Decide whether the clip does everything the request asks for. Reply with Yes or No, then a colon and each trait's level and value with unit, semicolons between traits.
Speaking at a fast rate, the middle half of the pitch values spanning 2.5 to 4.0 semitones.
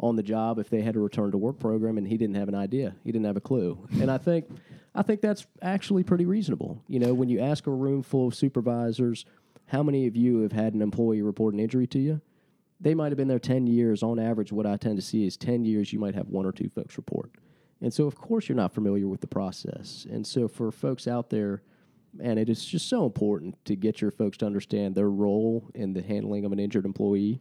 No: fast, 255 wpm; average, 4.4 semitones